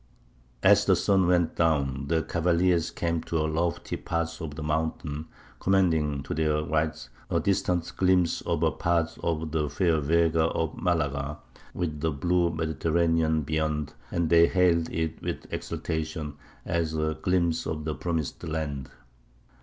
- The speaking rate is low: No, average, 150 wpm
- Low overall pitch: Yes, very low, 80 Hz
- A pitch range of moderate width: No, narrow, 1.6 semitones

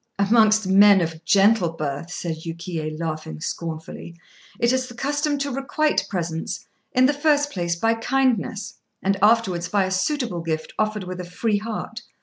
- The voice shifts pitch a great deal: Yes, wide, 5.8 semitones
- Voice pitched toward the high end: Yes, high, 200 Hz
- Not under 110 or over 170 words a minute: Yes, average, 160 wpm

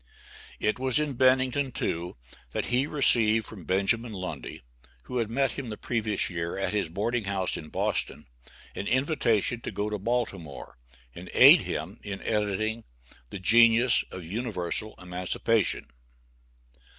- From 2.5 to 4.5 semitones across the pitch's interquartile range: Yes, average, 4.1 semitones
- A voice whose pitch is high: No, low, 110 Hz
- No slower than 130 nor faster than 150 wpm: Yes, average, 140 wpm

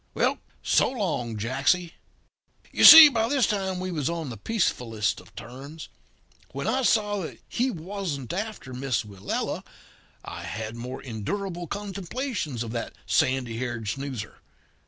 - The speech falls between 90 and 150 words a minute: Yes, average, 140 wpm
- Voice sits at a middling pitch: Yes, medium, 155 Hz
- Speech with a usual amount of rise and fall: No, wide, 9.0 semitones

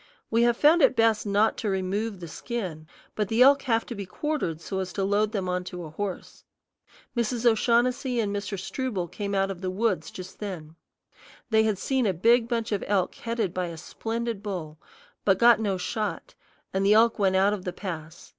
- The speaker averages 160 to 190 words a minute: No, fast, 205 wpm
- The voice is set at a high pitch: Yes, high, 205 Hz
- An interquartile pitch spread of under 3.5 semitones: No, average, 3.8 semitones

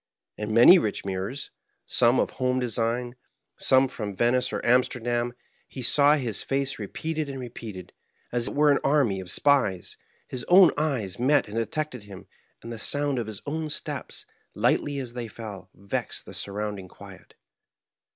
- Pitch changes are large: No, average, 4.6 semitones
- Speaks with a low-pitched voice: Yes, low, 120 Hz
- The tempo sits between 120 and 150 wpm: No, average, 165 wpm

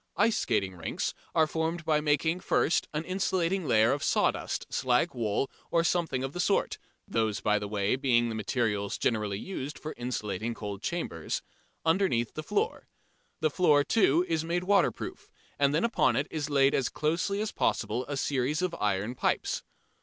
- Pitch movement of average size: No, wide, 6.7 semitones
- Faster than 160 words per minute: Yes, average, 170 wpm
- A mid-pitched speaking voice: Yes, medium, 145 Hz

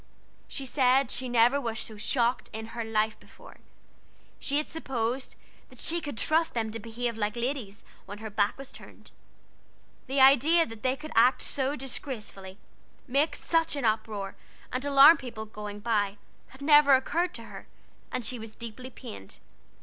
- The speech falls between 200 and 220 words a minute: No, average, 165 wpm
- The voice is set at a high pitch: Yes, high, 245 Hz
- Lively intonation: No, average, 4.1 semitones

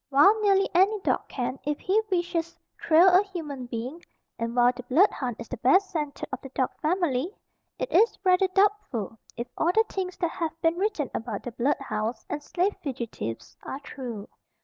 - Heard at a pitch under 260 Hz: No, very high, 310 Hz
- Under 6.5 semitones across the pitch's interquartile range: No, wide, 6.8 semitones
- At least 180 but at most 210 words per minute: Yes, average, 190 wpm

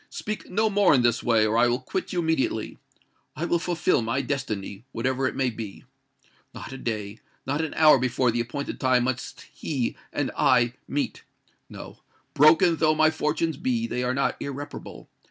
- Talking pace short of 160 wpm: No, average, 165 wpm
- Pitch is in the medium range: No, low, 130 Hz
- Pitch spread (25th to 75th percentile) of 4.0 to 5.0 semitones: Yes, average, 4.6 semitones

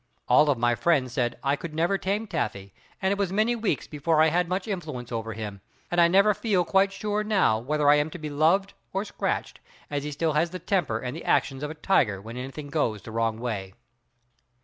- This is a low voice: No, medium, 150 Hz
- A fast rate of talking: Yes, fast, 225 wpm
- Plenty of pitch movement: Yes, wide, 7.6 semitones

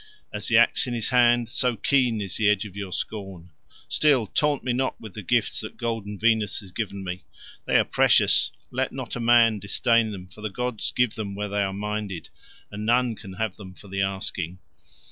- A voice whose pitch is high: No, low, 105 Hz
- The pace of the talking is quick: Yes, fast, 210 wpm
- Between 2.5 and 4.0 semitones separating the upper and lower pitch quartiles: Yes, average, 3.3 semitones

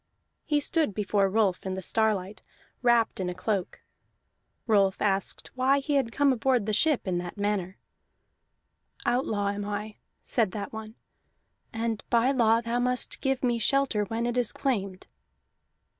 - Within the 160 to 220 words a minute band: No, average, 150 wpm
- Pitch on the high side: Yes, high, 220 Hz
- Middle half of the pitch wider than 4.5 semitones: No, average, 3.7 semitones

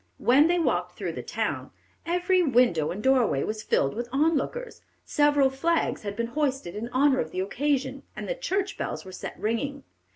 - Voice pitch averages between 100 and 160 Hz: No, very high, 270 Hz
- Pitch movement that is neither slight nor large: No, wide, 6.0 semitones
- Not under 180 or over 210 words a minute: Yes, average, 190 wpm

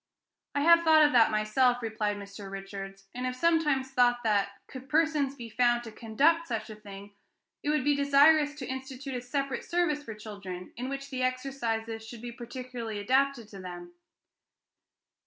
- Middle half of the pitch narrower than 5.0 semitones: Yes, average, 4.3 semitones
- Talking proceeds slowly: No, average, 175 wpm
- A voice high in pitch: Yes, very high, 250 Hz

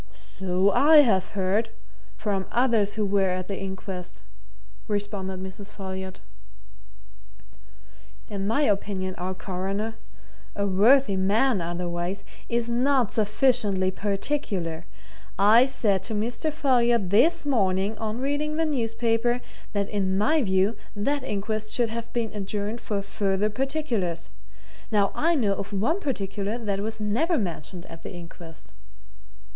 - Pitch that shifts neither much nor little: Yes, average, 3.7 semitones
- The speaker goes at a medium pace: No, slow, 130 wpm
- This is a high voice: Yes, high, 205 Hz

